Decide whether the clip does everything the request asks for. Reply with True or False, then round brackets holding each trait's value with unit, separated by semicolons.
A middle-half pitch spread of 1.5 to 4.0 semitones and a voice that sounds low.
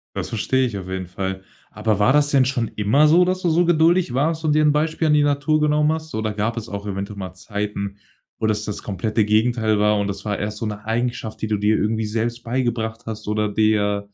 False (5.6 semitones; 110 Hz)